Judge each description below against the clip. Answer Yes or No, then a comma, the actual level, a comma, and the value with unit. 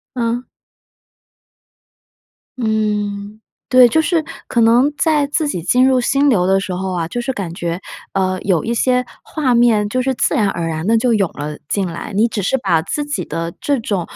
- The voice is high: Yes, high, 220 Hz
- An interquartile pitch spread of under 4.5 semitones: No, wide, 5.4 semitones